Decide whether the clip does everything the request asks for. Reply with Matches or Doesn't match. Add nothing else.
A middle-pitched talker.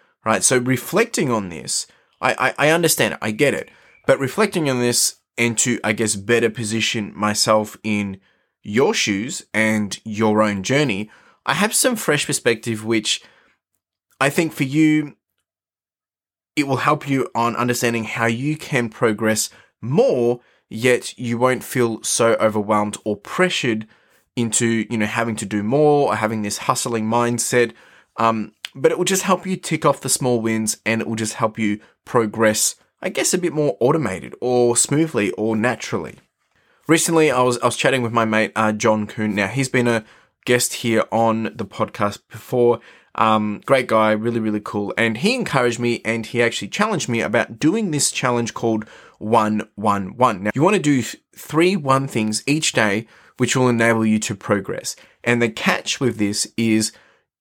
Doesn't match